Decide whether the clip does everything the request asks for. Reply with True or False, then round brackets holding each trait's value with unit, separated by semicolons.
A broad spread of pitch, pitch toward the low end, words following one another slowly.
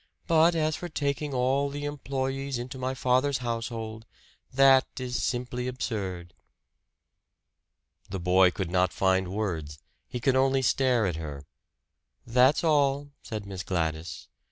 True (6.3 semitones; 125 Hz; 130 wpm)